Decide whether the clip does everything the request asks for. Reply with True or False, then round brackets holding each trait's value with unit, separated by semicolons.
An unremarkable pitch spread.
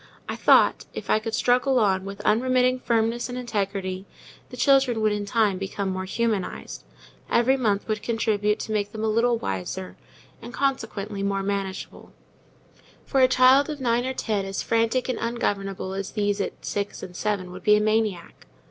True (3.4 semitones)